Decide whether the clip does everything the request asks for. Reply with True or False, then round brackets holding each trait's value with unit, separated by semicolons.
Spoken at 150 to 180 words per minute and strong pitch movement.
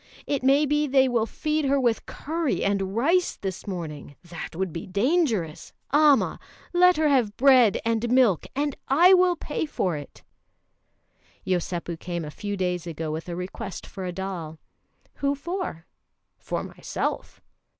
True (155 wpm; 8.4 semitones)